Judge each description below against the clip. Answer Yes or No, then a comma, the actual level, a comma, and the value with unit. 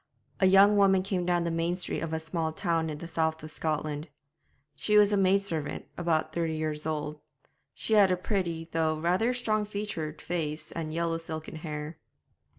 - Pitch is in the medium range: Yes, medium, 165 Hz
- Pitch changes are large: No, average, 3.2 semitones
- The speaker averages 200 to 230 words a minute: No, average, 185 wpm